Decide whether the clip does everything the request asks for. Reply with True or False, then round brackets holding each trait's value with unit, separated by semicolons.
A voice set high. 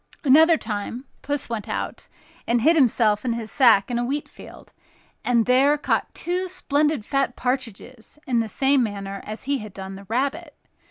True (250 Hz)